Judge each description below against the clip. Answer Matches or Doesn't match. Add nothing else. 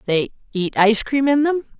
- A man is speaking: Doesn't match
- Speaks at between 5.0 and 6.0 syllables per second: Matches